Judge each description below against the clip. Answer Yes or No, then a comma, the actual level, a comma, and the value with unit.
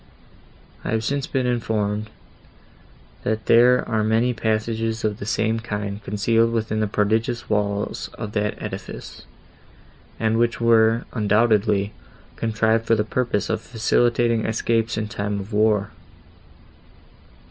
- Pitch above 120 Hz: No, low, 110 Hz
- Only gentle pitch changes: Yes, narrow, 1.7 semitones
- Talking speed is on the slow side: Yes, slow, 125 wpm